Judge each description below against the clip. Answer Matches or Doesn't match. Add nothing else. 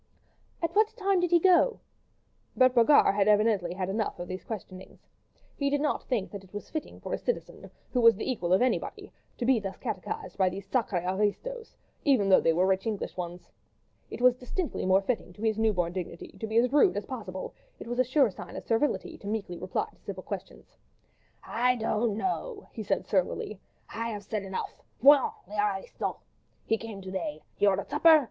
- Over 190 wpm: Matches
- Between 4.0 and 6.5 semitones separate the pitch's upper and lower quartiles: Matches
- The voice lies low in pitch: Doesn't match